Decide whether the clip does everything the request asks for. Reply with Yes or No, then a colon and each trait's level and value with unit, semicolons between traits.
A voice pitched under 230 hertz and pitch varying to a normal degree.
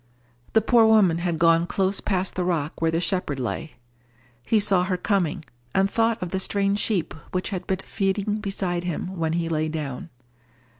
Yes: medium, 185 Hz; average, 3.1 semitones